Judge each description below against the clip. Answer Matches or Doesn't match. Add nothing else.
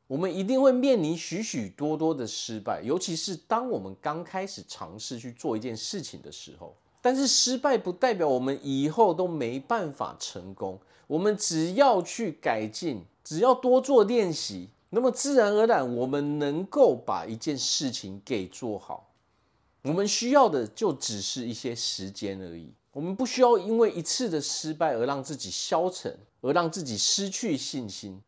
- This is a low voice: Doesn't match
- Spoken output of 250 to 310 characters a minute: Matches